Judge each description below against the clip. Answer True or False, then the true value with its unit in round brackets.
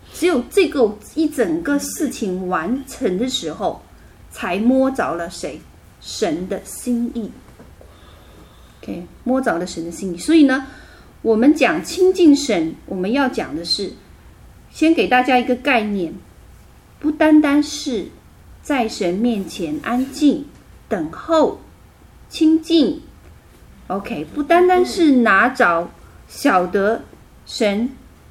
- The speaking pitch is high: True (250 Hz)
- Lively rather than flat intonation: True (7.3 semitones)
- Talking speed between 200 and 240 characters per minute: False (175 characters per minute)